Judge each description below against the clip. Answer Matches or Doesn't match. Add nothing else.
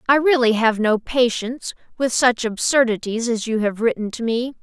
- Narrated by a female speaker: Matches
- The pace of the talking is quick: Doesn't match